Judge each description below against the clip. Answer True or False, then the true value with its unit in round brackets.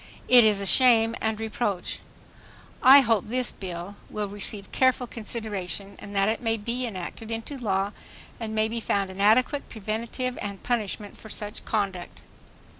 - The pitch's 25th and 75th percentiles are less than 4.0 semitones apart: True (2.8 semitones)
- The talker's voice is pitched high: True (220 Hz)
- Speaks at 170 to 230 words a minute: False (160 wpm)